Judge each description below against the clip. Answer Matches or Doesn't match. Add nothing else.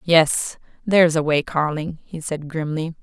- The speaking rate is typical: Matches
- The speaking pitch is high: Doesn't match